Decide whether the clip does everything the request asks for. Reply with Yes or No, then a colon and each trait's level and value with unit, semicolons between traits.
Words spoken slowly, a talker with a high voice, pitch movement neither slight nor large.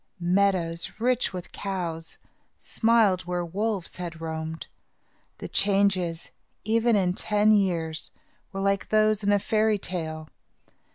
Yes: slow, 120 wpm; high, 195 Hz; average, 3.9 semitones